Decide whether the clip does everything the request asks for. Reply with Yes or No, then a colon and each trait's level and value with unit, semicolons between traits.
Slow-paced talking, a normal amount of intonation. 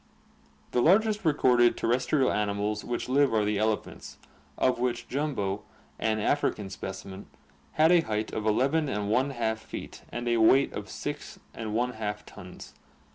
Yes: slow, 130 wpm; average, 4.2 semitones